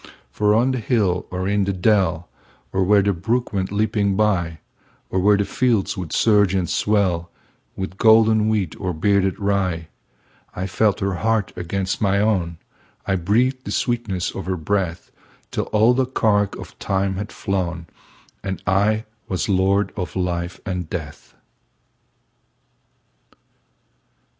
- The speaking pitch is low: Yes, low, 100 Hz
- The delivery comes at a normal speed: No, slow, 130 wpm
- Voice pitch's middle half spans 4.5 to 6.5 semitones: No, narrow, 2.6 semitones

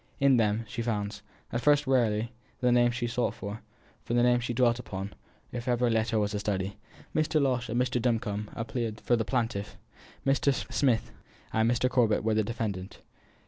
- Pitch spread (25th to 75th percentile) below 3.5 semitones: Yes, narrow, 2.4 semitones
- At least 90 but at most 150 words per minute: No, average, 185 wpm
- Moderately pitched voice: No, low, 115 Hz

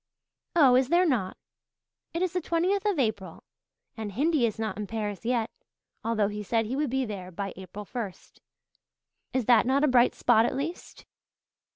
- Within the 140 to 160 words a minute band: No, average, 180 wpm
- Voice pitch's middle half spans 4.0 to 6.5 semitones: Yes, average, 5.2 semitones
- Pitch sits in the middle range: No, high, 240 Hz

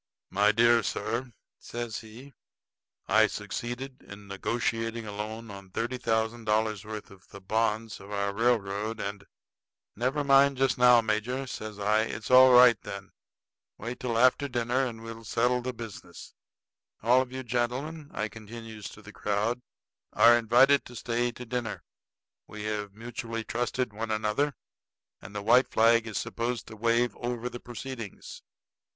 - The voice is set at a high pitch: No, low, 115 Hz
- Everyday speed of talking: Yes, average, 155 wpm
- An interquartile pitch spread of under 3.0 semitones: Yes, narrow, 2.4 semitones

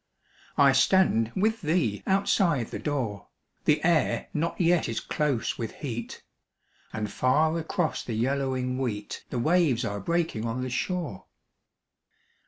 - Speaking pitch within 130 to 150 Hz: Yes, medium, 140 Hz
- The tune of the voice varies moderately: No, wide, 6.2 semitones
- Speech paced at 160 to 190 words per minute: No, slow, 135 wpm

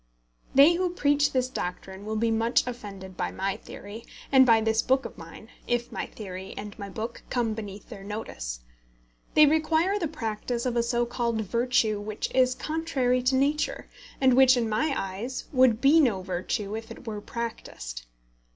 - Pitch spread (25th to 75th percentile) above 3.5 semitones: Yes, average, 4.0 semitones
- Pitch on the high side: Yes, high, 235 Hz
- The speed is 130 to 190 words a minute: Yes, average, 180 wpm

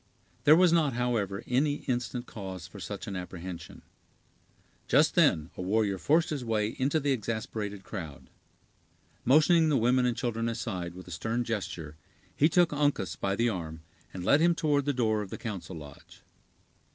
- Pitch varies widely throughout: Yes, wide, 6.8 semitones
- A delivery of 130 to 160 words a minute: No, average, 170 wpm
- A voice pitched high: No, low, 115 Hz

